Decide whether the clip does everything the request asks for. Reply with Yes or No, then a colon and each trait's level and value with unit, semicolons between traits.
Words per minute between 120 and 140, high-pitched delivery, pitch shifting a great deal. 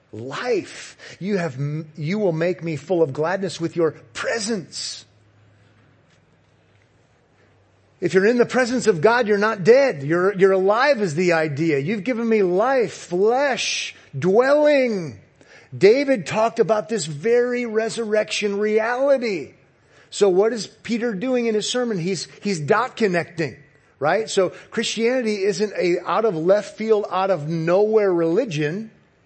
Yes: slow, 135 wpm; high, 195 Hz; wide, 5.9 semitones